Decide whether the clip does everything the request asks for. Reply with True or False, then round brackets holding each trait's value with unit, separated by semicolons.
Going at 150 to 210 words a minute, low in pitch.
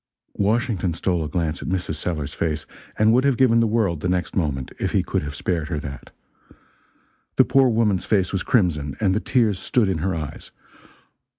True (195 wpm; 90 Hz)